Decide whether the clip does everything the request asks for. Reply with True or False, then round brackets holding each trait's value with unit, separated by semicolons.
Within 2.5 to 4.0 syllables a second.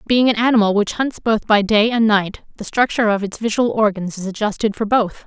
False (5.6 syllables/s)